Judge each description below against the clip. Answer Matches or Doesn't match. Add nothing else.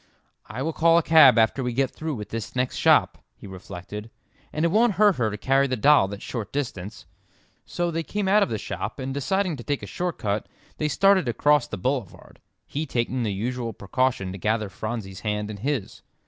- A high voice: Doesn't match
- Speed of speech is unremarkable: Doesn't match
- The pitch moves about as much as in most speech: Doesn't match